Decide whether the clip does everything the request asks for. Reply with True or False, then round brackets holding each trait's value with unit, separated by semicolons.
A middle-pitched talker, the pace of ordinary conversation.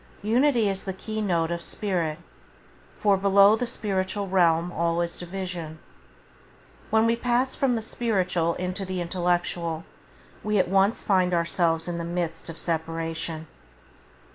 True (180 Hz; 150 wpm)